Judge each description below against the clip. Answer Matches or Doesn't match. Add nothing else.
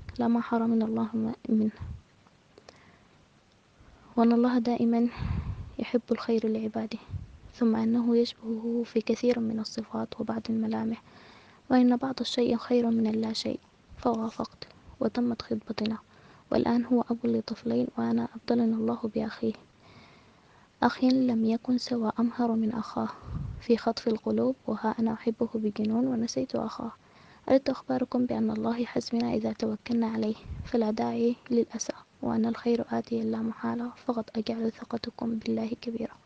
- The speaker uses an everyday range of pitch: Doesn't match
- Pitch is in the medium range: Doesn't match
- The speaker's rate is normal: Matches